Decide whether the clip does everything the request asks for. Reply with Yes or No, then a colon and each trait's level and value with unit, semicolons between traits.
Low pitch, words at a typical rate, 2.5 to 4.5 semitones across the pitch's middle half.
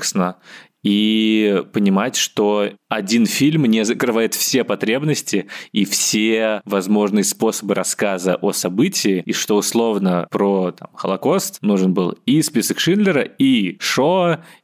Yes: low, 110 Hz; average, 120 wpm; average, 4.2 semitones